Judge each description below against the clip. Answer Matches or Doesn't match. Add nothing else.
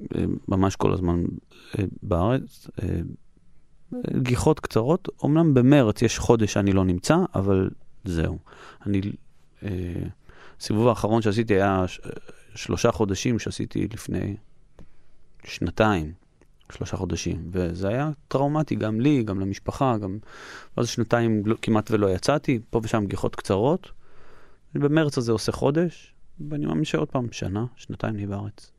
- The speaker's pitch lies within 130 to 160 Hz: Doesn't match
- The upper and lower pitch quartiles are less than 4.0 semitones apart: Doesn't match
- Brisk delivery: Doesn't match